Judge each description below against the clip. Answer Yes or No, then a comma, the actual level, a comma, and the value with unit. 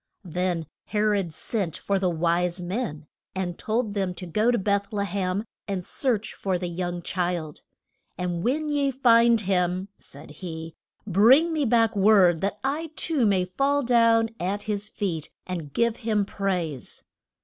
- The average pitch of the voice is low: No, high, 195 Hz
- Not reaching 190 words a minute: Yes, average, 160 wpm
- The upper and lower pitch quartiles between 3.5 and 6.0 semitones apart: Yes, average, 4.3 semitones